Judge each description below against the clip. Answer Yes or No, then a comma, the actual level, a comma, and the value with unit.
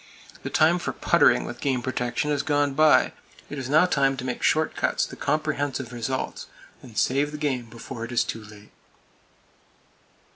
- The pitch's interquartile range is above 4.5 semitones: No, average, 3.5 semitones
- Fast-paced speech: No, average, 175 wpm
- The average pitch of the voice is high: No, low, 135 Hz